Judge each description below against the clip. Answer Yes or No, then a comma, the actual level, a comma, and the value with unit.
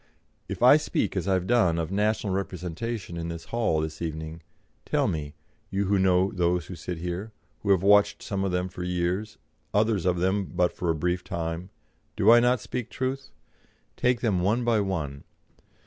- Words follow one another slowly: No, average, 190 wpm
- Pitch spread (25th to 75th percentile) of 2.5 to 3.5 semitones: Yes, average, 3.2 semitones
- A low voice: Yes, very low, 95 Hz